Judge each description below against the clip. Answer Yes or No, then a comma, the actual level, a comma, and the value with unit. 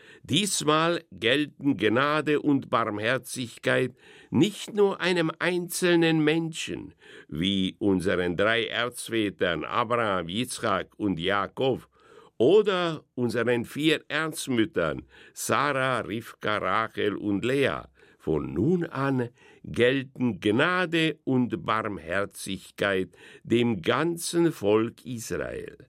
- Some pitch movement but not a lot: No, wide, 6.6 semitones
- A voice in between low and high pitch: No, low, 130 Hz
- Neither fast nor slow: No, slow, 90 wpm